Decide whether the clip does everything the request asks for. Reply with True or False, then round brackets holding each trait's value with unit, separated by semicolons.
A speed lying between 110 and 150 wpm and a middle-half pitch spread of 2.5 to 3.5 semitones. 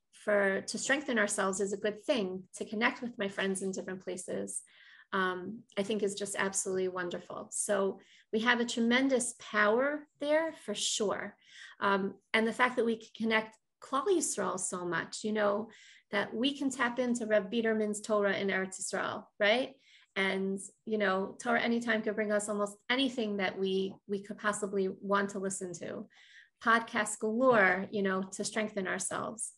False (170 wpm; 2.8 semitones)